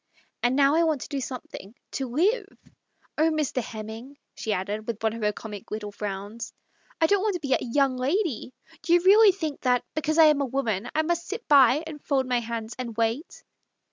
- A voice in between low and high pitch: No, very high, 265 Hz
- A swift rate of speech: Yes, fast, 235 wpm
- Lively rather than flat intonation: Yes, wide, 5.7 semitones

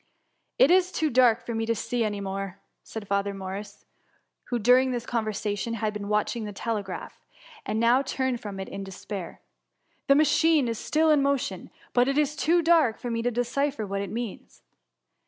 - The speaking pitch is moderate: No, high, 230 Hz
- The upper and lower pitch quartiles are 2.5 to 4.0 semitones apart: No, average, 4.6 semitones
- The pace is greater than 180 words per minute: Yes, average, 195 wpm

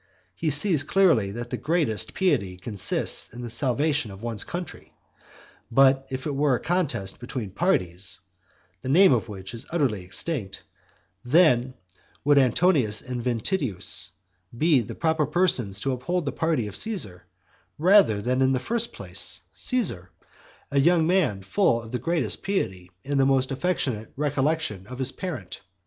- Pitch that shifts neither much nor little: No, wide, 6.8 semitones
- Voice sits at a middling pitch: No, low, 130 Hz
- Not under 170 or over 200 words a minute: No, average, 155 wpm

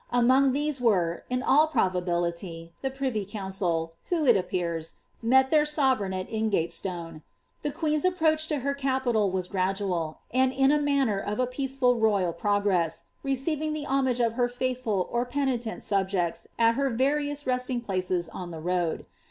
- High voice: Yes, high, 235 Hz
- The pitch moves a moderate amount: No, wide, 6.5 semitones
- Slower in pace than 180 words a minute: Yes, average, 160 wpm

